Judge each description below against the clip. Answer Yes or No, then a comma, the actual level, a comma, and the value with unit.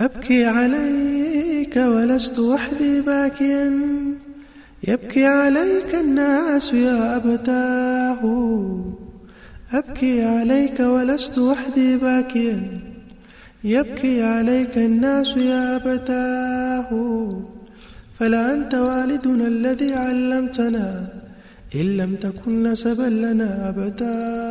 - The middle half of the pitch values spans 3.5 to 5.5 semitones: No, average, 2.9 semitones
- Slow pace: Yes, slow, 75 wpm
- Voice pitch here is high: Yes, very high, 250 Hz